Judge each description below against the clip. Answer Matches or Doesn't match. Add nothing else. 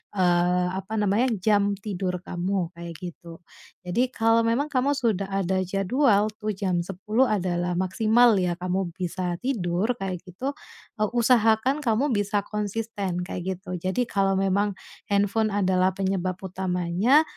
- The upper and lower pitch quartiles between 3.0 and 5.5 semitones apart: Matches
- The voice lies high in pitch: Matches